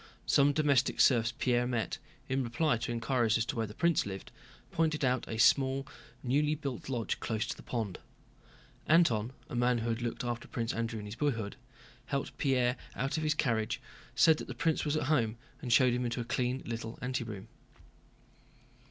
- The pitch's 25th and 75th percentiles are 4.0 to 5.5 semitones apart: No, average, 3.3 semitones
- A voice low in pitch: Yes, low, 125 Hz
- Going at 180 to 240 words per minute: Yes, average, 185 wpm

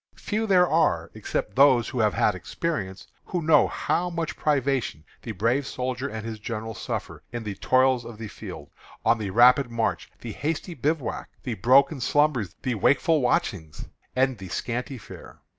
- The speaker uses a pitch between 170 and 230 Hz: No, low, 125 Hz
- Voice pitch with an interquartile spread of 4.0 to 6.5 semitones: Yes, average, 4.6 semitones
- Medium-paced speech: Yes, average, 170 wpm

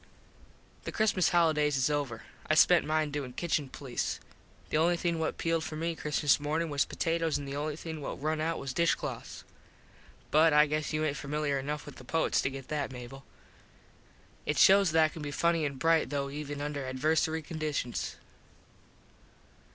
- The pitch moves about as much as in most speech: No, narrow, 2.3 semitones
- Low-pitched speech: No, medium, 150 Hz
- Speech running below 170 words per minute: No, average, 180 wpm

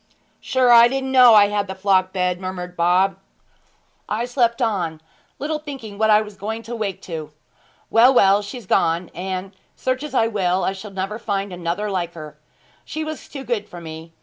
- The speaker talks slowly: No, average, 190 wpm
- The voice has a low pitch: No, high, 200 Hz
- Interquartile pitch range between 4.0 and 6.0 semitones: Yes, average, 4.3 semitones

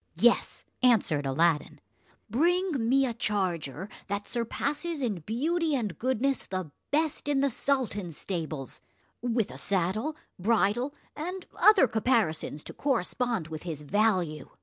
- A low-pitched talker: No, high, 225 Hz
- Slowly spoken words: Yes, slow, 125 wpm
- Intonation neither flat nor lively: No, wide, 7.5 semitones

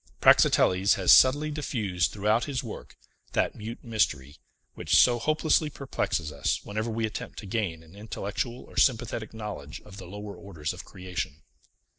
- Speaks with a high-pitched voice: No, low, 105 Hz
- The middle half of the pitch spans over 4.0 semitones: Yes, average, 4.4 semitones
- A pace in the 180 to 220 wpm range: No, average, 155 wpm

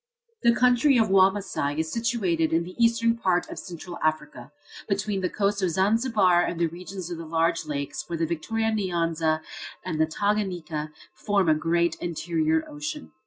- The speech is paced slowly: No, average, 165 wpm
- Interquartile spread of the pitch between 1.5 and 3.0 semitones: No, average, 4.1 semitones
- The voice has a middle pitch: Yes, medium, 175 Hz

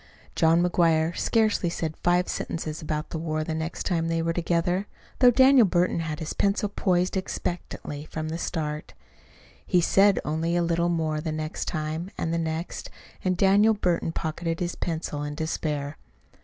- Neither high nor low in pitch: Yes, medium, 165 Hz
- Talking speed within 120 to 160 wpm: No, average, 170 wpm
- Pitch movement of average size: No, narrow, 2.2 semitones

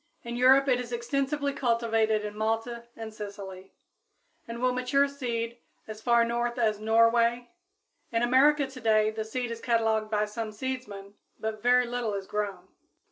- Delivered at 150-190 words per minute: Yes, average, 155 wpm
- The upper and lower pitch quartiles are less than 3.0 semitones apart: Yes, narrow, 2.4 semitones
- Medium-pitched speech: No, high, 230 Hz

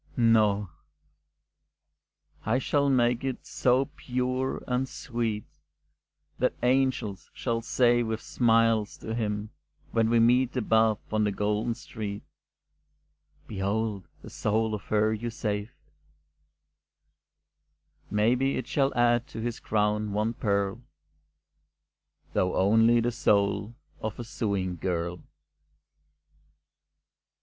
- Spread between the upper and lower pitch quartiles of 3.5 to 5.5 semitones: No, narrow, 2.5 semitones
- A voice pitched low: Yes, low, 110 Hz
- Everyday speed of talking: No, slow, 105 wpm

